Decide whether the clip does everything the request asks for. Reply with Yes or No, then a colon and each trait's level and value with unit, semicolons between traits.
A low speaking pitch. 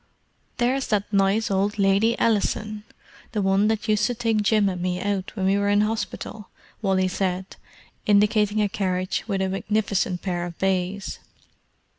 No: high, 200 Hz